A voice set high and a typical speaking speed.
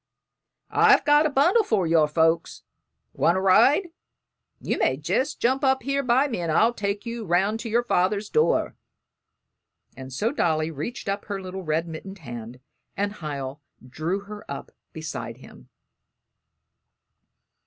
Yes: high, 195 Hz; average, 150 wpm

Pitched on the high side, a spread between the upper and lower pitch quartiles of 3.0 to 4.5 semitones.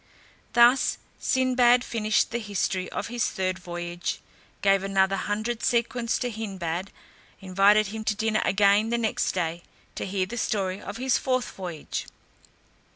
Yes: high, 205 Hz; average, 3.8 semitones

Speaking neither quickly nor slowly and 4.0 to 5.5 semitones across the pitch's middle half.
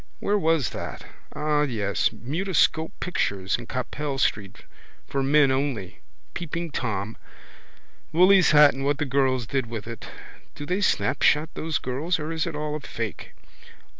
Yes: average, 150 wpm; average, 4.6 semitones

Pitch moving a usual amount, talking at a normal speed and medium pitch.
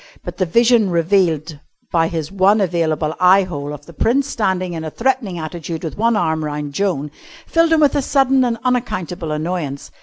No: wide, 6.3 semitones; average, 185 wpm; medium, 180 Hz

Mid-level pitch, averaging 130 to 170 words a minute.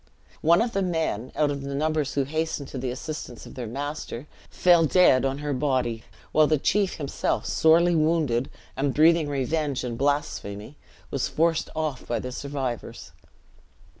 Yes: medium, 145 Hz; average, 165 wpm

